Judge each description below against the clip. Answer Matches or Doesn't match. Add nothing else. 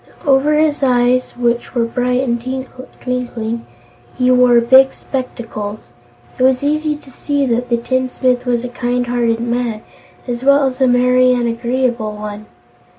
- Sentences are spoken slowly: Doesn't match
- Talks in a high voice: Matches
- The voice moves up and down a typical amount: Doesn't match